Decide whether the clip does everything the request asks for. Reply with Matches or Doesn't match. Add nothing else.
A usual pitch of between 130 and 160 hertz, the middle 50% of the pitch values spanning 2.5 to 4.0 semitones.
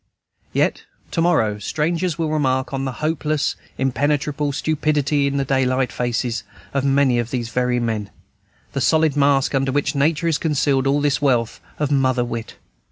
Matches